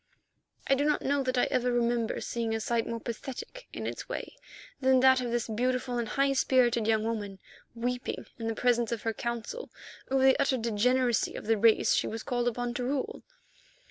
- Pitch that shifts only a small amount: Yes, narrow, 2.2 semitones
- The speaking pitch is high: Yes, high, 245 Hz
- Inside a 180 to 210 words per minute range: Yes, average, 200 wpm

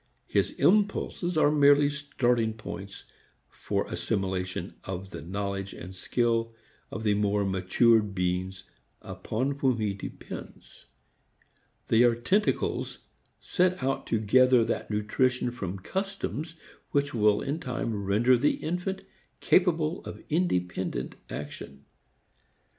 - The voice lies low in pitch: Yes, low, 115 Hz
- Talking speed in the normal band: No, slow, 115 wpm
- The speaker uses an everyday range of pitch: No, wide, 6.5 semitones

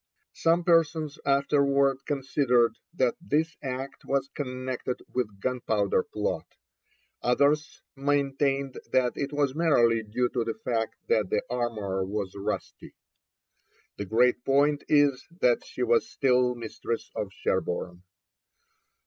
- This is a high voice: No, low, 130 Hz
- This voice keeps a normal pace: No, slow, 120 wpm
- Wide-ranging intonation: No, average, 3.4 semitones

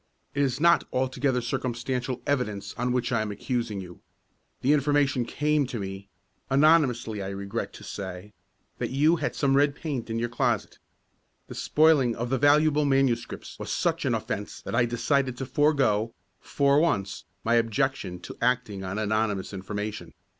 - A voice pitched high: No, low, 125 Hz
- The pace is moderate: Yes, average, 160 wpm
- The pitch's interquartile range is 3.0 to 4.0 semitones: No, average, 4.6 semitones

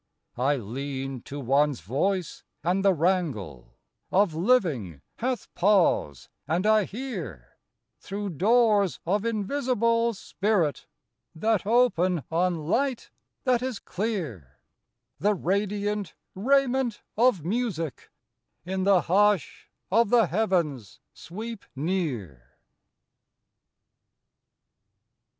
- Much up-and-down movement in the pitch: Yes, wide, 6.7 semitones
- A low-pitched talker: No, high, 190 Hz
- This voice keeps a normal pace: No, slow, 95 wpm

